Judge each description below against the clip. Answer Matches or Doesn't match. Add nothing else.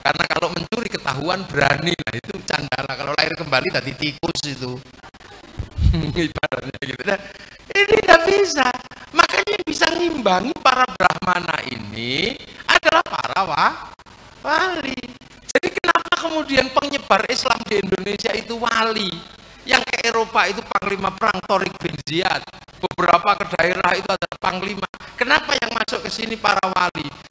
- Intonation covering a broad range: Matches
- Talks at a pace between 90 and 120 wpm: Doesn't match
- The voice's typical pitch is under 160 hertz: Doesn't match